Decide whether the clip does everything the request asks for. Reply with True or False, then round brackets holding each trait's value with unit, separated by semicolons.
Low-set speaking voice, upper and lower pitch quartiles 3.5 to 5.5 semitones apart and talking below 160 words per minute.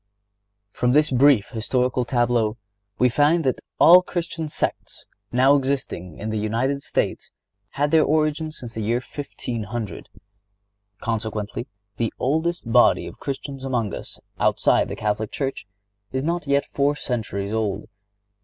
True (125 Hz; 4.4 semitones; 145 wpm)